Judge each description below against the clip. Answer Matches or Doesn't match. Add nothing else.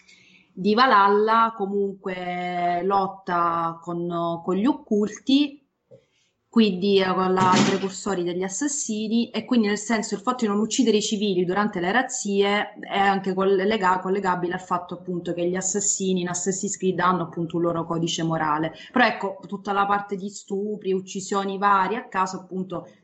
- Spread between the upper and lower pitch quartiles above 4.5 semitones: Doesn't match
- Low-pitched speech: Doesn't match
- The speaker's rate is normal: Matches